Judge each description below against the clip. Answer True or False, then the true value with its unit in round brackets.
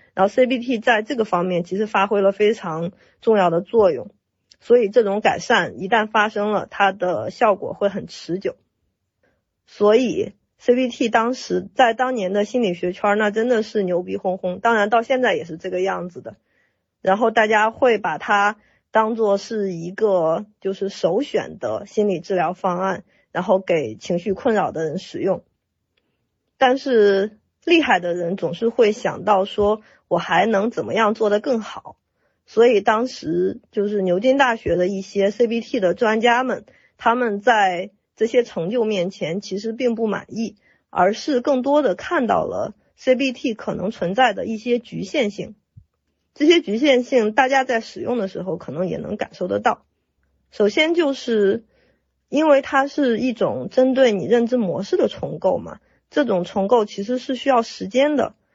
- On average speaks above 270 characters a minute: False (250 characters per minute)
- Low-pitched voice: False (215 Hz)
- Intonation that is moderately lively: True (4.5 semitones)